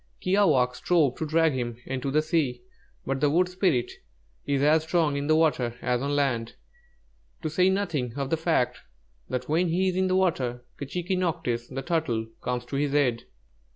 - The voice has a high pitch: No, medium, 145 Hz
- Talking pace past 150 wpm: Yes, average, 185 wpm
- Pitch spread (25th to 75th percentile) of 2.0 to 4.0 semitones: No, average, 4.8 semitones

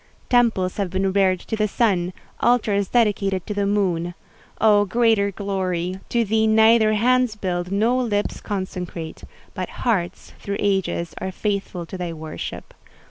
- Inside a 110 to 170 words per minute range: Yes, average, 140 wpm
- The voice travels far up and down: No, average, 3.0 semitones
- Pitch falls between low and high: No, high, 200 Hz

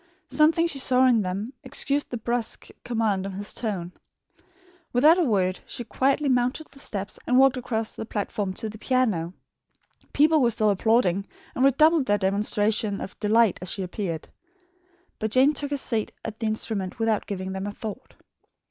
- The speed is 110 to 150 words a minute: No, average, 175 wpm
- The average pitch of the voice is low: No, high, 220 Hz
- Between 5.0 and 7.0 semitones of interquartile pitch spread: No, average, 4.3 semitones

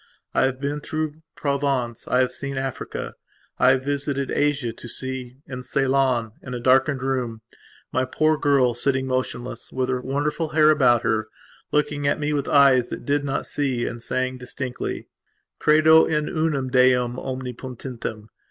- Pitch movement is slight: Yes, narrow, 2.2 semitones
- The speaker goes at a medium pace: Yes, average, 160 wpm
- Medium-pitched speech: No, low, 130 Hz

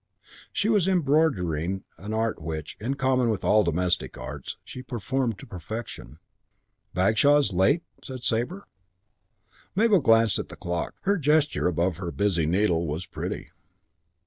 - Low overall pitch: Yes, low, 110 Hz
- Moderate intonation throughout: No, wide, 7.9 semitones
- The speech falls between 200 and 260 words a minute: No, average, 145 wpm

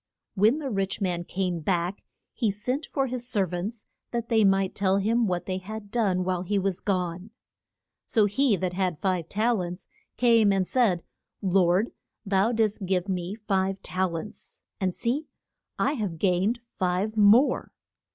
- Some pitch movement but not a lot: Yes, average, 3.3 semitones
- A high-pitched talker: Yes, high, 195 Hz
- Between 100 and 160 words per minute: No, average, 170 wpm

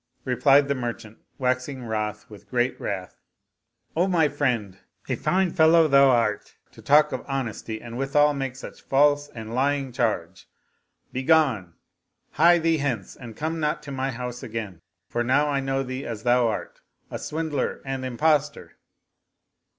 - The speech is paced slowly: No, average, 160 wpm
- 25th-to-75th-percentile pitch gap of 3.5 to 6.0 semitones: Yes, average, 3.8 semitones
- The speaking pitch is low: Yes, low, 130 Hz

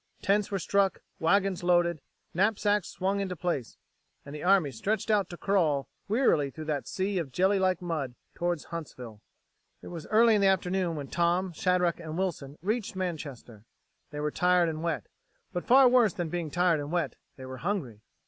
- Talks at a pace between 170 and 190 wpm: Yes, average, 180 wpm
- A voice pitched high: No, medium, 175 Hz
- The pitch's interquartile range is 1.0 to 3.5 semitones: No, average, 4.1 semitones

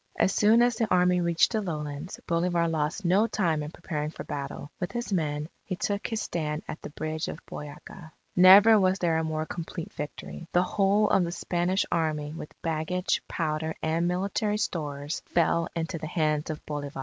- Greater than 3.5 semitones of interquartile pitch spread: No, average, 3.2 semitones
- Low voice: No, medium, 170 Hz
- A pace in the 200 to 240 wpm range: No, average, 185 wpm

